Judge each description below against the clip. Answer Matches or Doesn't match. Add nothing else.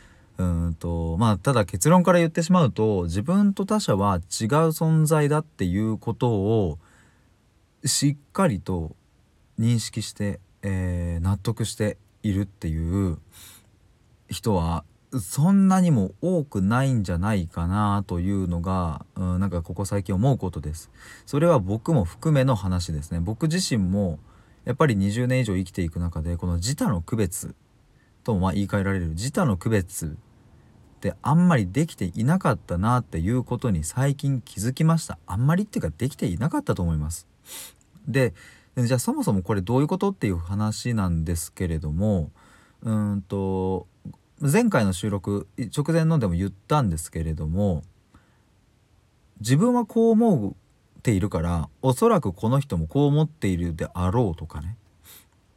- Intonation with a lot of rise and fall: Matches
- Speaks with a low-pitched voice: Matches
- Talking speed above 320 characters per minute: Doesn't match